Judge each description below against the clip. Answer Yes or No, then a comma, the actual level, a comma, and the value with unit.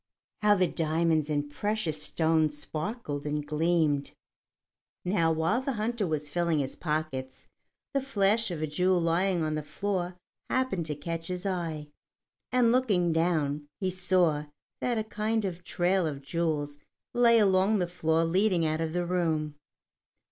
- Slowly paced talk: No, average, 155 wpm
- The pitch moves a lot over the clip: No, average, 4.0 semitones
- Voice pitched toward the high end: No, medium, 170 Hz